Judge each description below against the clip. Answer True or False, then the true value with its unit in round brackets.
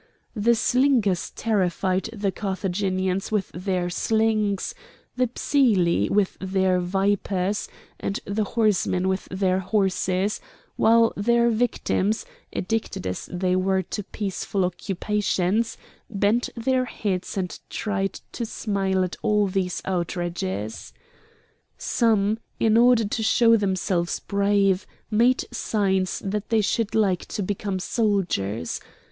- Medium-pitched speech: False (200 Hz)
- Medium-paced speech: False (115 wpm)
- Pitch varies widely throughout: False (2.9 semitones)